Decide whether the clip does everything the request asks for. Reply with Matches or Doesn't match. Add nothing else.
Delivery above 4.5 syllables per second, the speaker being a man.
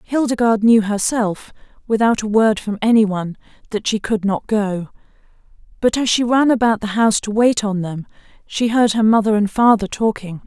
Doesn't match